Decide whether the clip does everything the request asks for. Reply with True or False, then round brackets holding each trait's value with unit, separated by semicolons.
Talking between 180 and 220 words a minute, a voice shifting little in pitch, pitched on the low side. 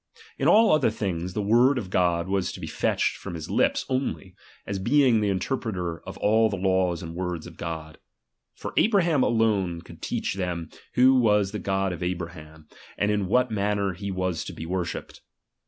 False (190 wpm; 4.0 semitones; 95 Hz)